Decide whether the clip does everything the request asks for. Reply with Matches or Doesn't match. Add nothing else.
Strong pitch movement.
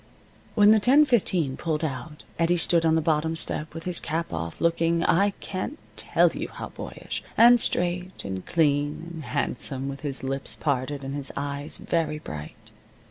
Doesn't match